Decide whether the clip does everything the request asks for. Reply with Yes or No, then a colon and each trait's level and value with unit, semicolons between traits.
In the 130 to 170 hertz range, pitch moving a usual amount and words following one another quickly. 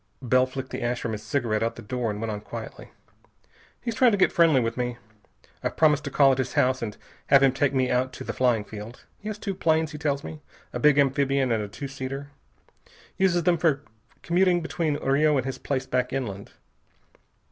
Yes: low, 135 Hz; average, 3.8 semitones; fast, 215 wpm